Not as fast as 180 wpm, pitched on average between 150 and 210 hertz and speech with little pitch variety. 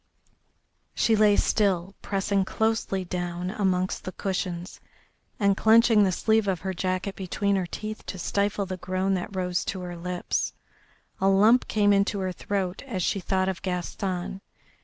Yes: average, 160 wpm; high, 190 Hz; narrow, 1.9 semitones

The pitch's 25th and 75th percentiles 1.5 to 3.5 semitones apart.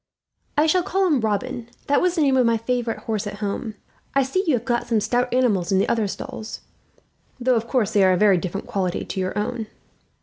No: average, 3.9 semitones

